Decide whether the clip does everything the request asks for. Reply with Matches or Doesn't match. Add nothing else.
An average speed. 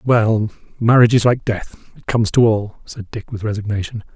Matches